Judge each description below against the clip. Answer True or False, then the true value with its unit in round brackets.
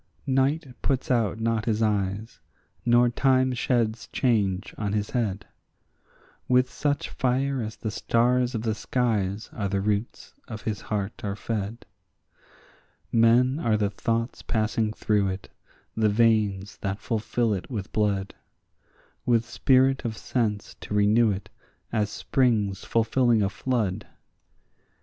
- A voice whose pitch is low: True (110 Hz)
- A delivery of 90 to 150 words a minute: True (135 wpm)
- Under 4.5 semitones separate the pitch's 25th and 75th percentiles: True (2.9 semitones)